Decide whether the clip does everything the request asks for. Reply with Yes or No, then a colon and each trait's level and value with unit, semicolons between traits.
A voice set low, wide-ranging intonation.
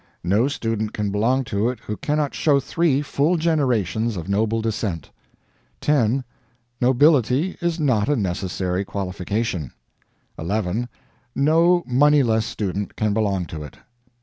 Yes: low, 115 Hz; wide, 5.9 semitones